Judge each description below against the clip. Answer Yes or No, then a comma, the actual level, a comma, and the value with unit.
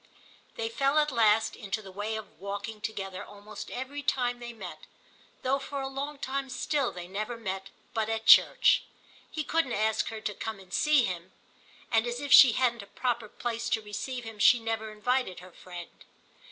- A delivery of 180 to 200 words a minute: Yes, average, 190 wpm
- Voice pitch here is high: Yes, high, 225 Hz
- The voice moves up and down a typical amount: Yes, average, 3.7 semitones